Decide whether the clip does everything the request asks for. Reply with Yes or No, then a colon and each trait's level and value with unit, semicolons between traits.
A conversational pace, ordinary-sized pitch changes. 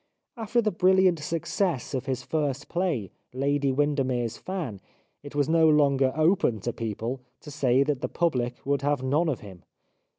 Yes: average, 170 wpm; average, 4.2 semitones